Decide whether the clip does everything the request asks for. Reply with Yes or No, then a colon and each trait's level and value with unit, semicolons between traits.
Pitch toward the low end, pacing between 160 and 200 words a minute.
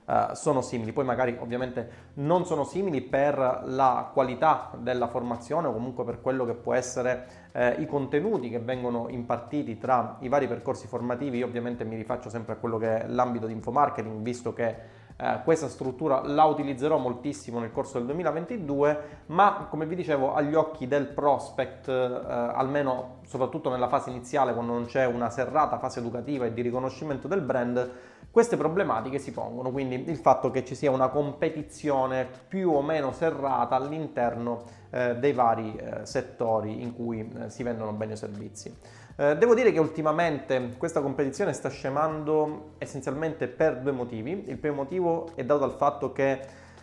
Yes: low, 130 Hz; fast, 170 wpm